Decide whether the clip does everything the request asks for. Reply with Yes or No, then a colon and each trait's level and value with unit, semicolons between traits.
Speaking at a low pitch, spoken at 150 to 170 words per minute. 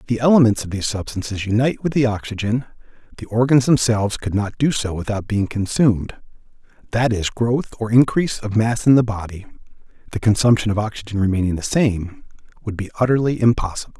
Yes: low, 110 Hz; average, 165 wpm